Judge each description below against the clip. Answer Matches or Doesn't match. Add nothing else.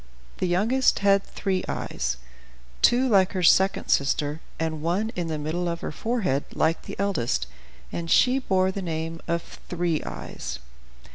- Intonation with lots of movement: Doesn't match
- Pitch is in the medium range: Matches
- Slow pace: Doesn't match